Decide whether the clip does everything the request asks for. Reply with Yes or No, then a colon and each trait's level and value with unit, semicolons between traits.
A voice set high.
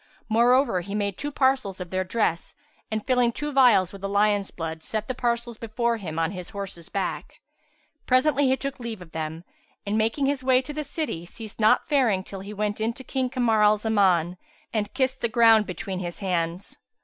Yes: high, 215 Hz